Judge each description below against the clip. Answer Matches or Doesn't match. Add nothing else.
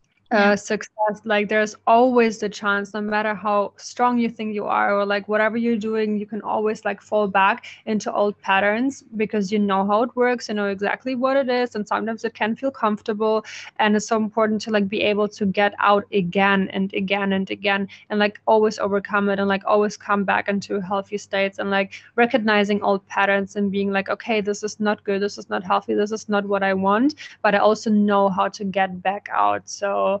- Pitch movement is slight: Matches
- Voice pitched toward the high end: Matches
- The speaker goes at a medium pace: Doesn't match